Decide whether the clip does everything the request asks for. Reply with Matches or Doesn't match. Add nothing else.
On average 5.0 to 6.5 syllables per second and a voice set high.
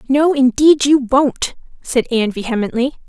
Doesn't match